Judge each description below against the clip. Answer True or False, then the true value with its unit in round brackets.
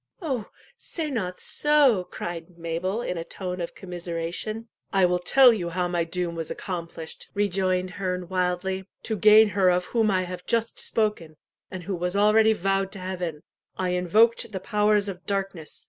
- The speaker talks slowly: False (170 wpm)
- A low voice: False (185 Hz)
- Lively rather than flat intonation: False (2.9 semitones)